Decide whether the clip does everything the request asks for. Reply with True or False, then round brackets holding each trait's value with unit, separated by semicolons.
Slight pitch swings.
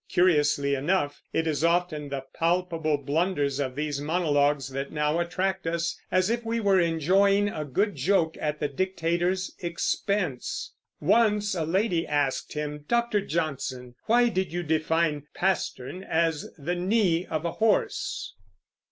False (4.3 semitones)